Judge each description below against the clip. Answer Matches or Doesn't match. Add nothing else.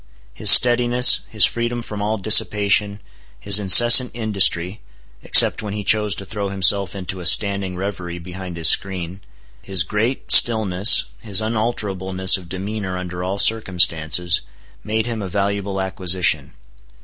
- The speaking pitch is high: Doesn't match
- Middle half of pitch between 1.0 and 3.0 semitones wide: Matches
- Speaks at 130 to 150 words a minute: Matches